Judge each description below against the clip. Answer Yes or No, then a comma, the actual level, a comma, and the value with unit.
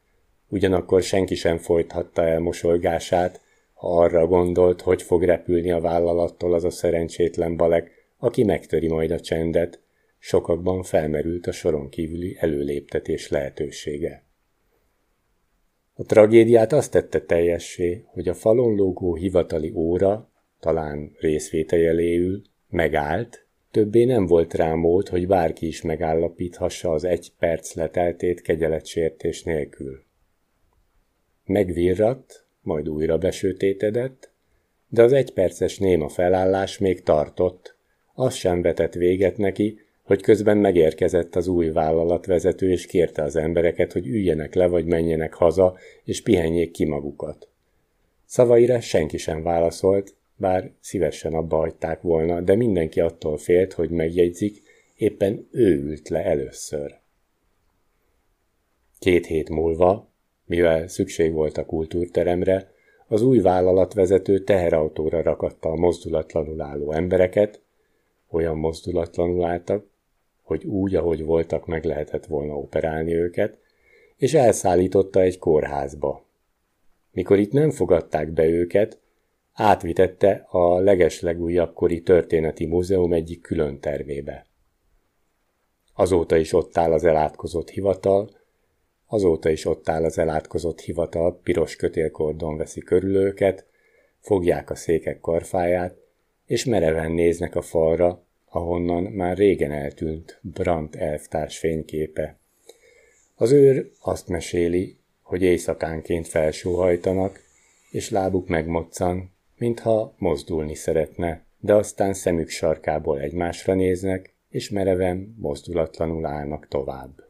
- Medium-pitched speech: No, very low, 90 Hz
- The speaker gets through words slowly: No, average, 115 wpm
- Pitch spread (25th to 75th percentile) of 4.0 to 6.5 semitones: No, average, 2.8 semitones